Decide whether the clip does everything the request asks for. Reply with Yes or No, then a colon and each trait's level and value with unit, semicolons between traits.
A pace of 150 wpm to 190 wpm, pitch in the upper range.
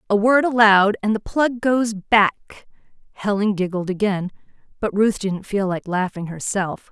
Yes: average, 155 wpm; high, 205 Hz